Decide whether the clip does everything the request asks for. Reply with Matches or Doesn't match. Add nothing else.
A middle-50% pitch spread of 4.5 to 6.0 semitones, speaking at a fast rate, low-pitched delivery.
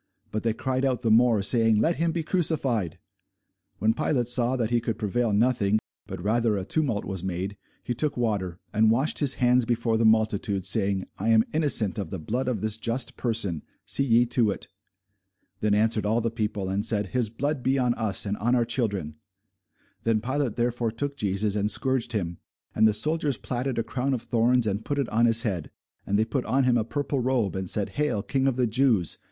Doesn't match